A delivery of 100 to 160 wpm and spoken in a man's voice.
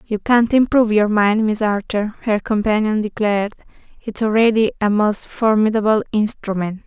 No: average, 140 wpm; female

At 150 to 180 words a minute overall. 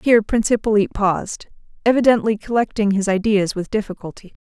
No: slow, 135 wpm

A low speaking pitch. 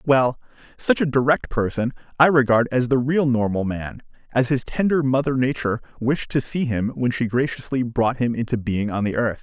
Yes: low, 125 Hz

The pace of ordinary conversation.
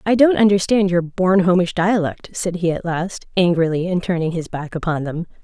Yes: average, 190 wpm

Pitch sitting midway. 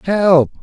Yes: medium, 175 Hz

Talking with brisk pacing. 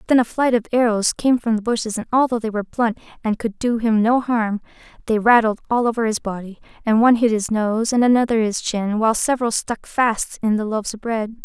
Yes: fast, 230 wpm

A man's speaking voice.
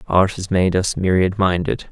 Yes: male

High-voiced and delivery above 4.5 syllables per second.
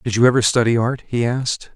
No: low, 120 Hz; 6.2 syllables/s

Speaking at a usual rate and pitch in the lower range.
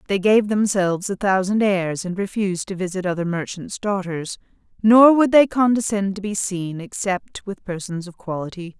No: average, 170 wpm; high, 195 Hz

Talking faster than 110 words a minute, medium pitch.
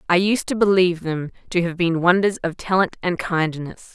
Yes: average, 200 wpm; medium, 175 Hz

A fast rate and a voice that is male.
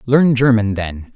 No: average, 155 wpm; male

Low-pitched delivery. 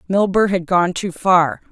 No: medium, 185 Hz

